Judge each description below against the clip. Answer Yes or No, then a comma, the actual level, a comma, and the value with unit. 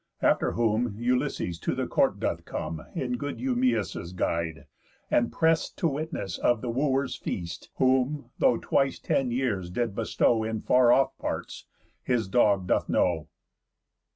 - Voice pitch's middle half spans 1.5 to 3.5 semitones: No, average, 5.2 semitones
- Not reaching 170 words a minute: Yes, average, 150 wpm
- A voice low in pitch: Yes, low, 120 Hz